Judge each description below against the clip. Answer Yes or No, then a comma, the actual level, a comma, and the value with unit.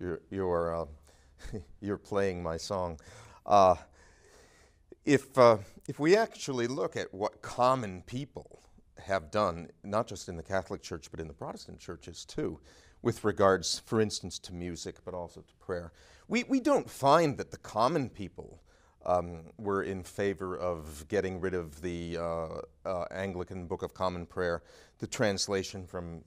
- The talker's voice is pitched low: Yes, very low, 95 Hz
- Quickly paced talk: No, average, 160 wpm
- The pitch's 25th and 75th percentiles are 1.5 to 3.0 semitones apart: No, average, 3.5 semitones